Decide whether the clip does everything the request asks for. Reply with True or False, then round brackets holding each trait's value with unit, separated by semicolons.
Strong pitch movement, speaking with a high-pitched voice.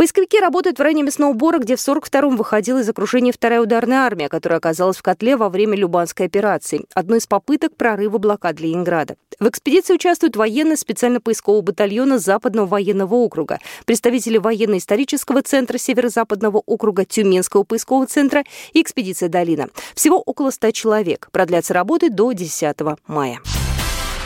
True (5.7 semitones; 225 Hz)